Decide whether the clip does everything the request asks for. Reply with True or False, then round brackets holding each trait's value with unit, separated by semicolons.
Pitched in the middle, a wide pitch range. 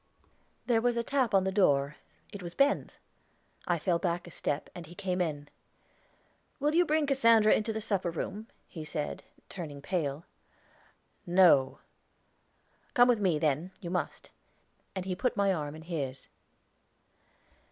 True (180 Hz; 5.8 semitones)